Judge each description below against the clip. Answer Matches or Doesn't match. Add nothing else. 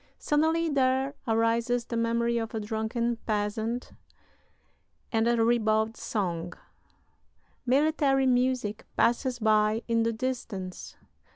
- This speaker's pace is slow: Matches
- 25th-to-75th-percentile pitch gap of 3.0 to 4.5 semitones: Doesn't match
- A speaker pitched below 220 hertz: Doesn't match